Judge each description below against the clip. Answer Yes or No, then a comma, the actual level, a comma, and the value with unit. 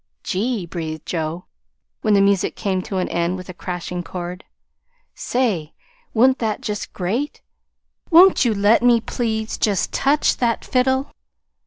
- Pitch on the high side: Yes, high, 205 Hz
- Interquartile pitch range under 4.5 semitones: No, average, 5.1 semitones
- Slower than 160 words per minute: Yes, average, 145 wpm